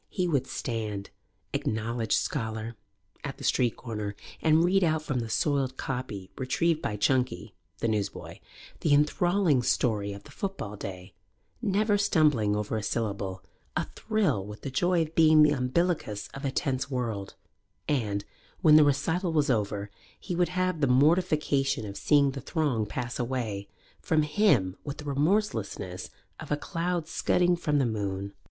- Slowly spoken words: No, average, 155 wpm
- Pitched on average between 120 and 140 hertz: Yes, low, 135 Hz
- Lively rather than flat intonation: Yes, wide, 6.7 semitones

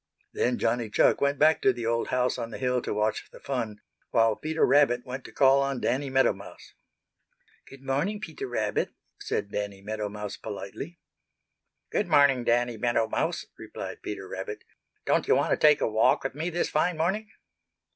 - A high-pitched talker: No, low, 125 Hz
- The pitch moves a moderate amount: Yes, average, 4.8 semitones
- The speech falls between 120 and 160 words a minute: No, average, 185 wpm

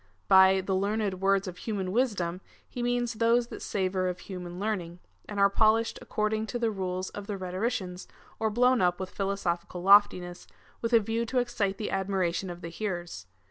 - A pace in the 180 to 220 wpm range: Yes, average, 185 wpm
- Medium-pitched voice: No, high, 195 Hz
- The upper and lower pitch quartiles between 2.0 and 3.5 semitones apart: Yes, average, 3.2 semitones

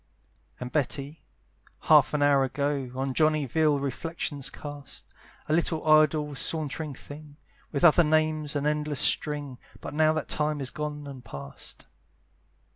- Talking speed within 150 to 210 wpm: No, average, 140 wpm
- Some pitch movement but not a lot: No, narrow, 1.8 semitones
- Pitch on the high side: No, medium, 150 Hz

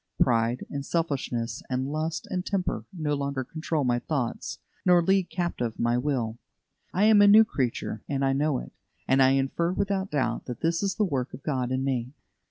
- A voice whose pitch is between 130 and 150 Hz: Yes, medium, 140 Hz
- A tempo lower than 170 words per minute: No, average, 190 wpm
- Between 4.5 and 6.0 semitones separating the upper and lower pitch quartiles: Yes, average, 5.3 semitones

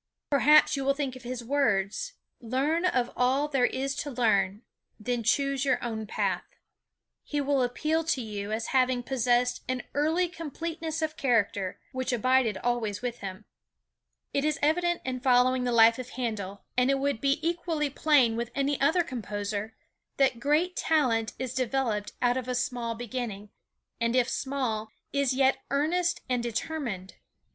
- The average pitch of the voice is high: Yes, very high, 255 Hz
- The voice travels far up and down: No, average, 3.5 semitones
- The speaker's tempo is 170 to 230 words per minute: No, average, 160 wpm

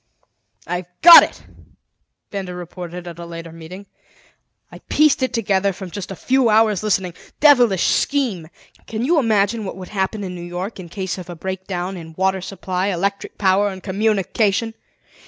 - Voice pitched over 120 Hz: Yes, high, 190 Hz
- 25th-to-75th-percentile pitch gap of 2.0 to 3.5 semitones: Yes, average, 3.1 semitones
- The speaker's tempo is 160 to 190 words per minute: Yes, average, 165 wpm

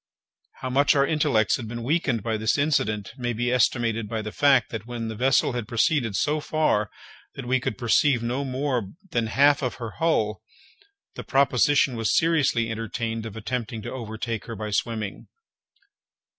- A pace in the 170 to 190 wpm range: Yes, average, 175 wpm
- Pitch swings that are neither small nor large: Yes, average, 3.4 semitones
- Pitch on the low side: Yes, low, 120 Hz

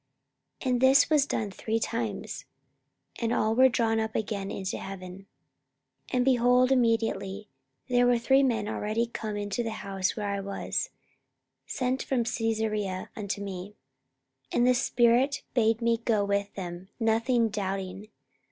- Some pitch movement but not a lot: Yes, average, 3.3 semitones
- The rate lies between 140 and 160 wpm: Yes, average, 150 wpm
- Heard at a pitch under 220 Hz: No, high, 225 Hz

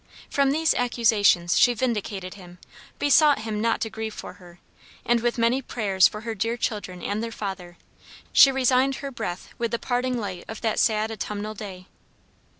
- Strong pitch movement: No, average, 3.4 semitones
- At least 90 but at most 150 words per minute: No, average, 175 wpm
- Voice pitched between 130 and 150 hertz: No, high, 220 Hz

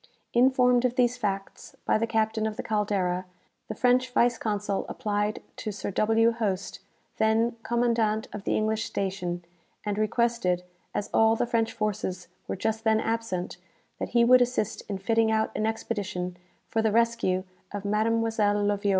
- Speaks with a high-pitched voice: Yes, high, 220 Hz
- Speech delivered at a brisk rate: No, average, 160 wpm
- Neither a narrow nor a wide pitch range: No, narrow, 2.1 semitones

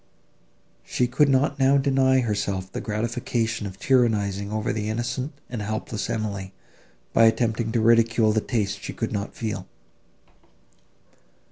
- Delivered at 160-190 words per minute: No, slow, 135 wpm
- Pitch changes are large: No, average, 2.8 semitones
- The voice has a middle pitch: No, low, 115 Hz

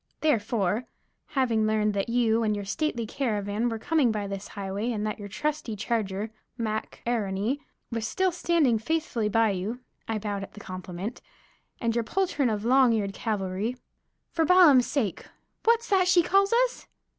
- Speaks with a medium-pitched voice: No, high, 225 Hz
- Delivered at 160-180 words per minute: Yes, average, 165 wpm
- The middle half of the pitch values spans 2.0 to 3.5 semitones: No, average, 4.8 semitones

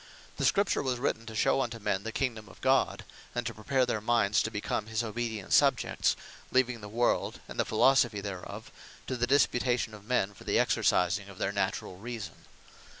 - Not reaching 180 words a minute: No, average, 190 wpm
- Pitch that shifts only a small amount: No, average, 3.1 semitones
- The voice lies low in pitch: Yes, low, 115 Hz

